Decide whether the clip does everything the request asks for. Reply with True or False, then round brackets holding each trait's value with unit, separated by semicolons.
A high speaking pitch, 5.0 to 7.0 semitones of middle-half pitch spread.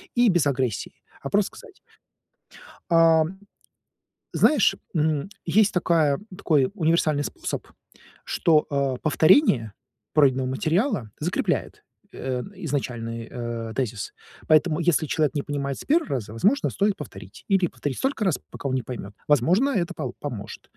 False (150 Hz; 5.6 semitones)